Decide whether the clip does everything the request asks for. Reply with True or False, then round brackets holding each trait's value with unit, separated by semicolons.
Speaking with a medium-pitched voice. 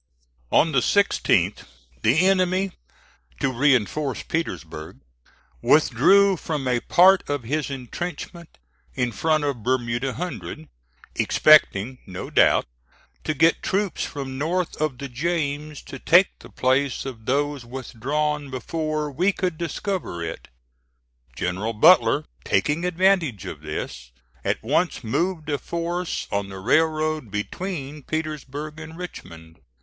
True (145 Hz)